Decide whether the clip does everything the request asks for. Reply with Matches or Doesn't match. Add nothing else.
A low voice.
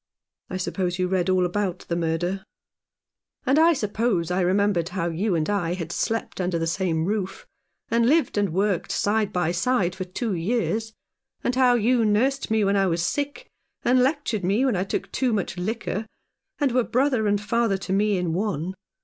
Doesn't match